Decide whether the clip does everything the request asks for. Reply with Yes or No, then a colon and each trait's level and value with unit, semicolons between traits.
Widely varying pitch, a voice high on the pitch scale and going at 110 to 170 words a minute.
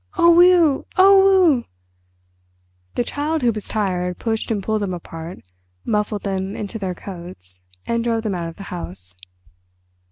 Yes: wide, 6.3 semitones; high, 210 Hz; average, 155 wpm